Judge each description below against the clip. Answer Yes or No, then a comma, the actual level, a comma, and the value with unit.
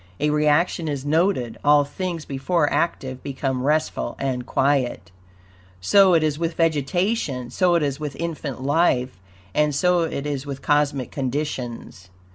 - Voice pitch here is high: No, medium, 145 Hz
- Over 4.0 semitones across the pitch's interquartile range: No, average, 3.7 semitones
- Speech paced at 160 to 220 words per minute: No, average, 145 wpm